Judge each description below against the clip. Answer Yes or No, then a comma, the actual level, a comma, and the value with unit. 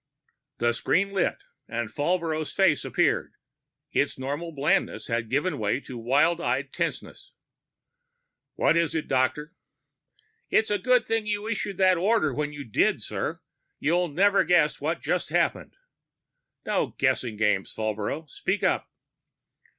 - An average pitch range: No, wide, 6.4 semitones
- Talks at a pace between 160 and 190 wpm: No, average, 140 wpm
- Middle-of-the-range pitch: Yes, medium, 155 Hz